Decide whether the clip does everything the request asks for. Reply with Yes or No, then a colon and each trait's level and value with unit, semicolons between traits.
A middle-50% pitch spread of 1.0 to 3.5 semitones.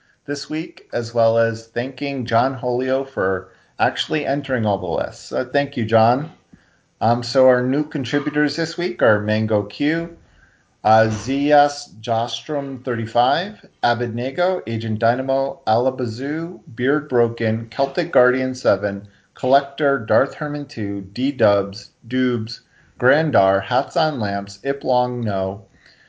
No: average, 4.0 semitones